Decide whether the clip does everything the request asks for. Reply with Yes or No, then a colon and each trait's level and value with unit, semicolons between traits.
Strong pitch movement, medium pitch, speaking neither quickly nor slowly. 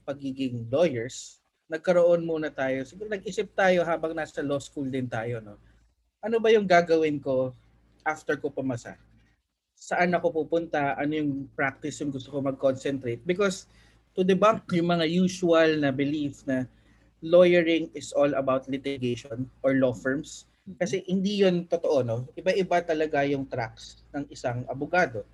No: average, 4.8 semitones; medium, 145 Hz; average, 145 wpm